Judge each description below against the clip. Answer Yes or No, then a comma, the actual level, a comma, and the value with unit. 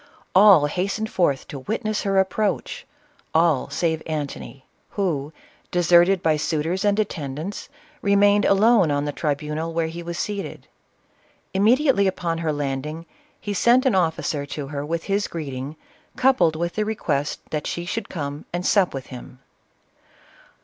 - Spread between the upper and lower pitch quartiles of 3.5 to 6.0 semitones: Yes, average, 5.1 semitones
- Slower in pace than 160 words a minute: Yes, average, 150 wpm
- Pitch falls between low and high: Yes, medium, 170 Hz